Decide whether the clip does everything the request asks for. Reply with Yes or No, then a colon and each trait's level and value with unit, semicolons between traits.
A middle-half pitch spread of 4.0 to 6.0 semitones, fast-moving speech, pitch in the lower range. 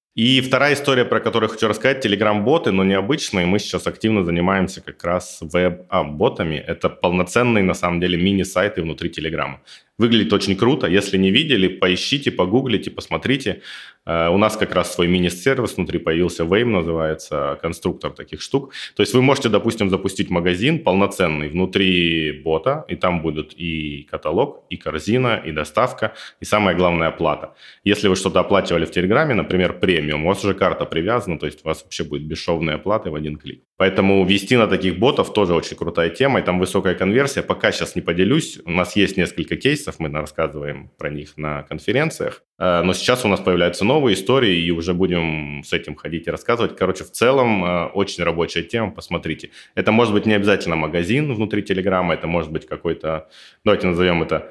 No: average, 3.6 semitones; fast, 175 wpm; very low, 90 Hz